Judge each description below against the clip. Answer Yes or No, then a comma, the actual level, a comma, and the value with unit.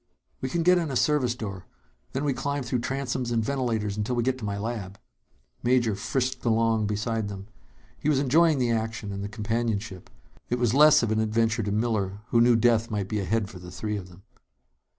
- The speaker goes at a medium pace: No, fast, 210 wpm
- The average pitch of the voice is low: Yes, low, 115 Hz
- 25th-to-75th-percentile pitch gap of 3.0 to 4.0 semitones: Yes, average, 3.3 semitones